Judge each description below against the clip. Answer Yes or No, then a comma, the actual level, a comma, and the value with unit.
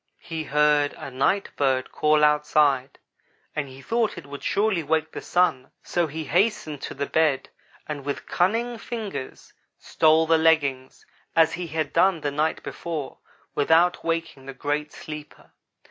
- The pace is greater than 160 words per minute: No, average, 155 wpm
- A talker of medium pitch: Yes, medium, 155 Hz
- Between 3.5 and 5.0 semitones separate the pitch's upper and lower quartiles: No, average, 2.8 semitones